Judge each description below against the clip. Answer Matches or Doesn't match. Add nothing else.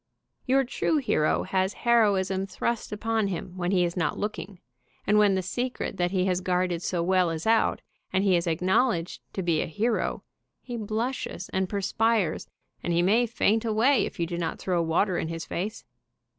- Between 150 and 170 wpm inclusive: Doesn't match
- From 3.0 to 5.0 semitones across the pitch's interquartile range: Matches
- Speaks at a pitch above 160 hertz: Matches